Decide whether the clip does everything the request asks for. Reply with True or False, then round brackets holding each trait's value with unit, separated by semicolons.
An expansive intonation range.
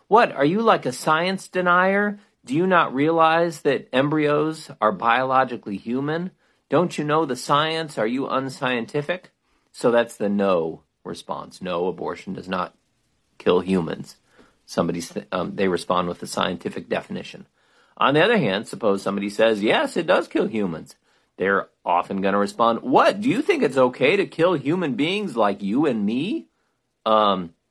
True (7.8 semitones)